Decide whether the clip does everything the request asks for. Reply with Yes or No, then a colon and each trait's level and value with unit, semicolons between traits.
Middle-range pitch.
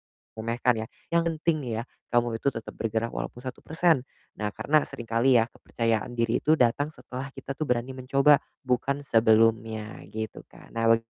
No: low, 120 Hz